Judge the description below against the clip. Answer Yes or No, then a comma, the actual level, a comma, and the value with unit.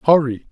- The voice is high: No, medium, 140 Hz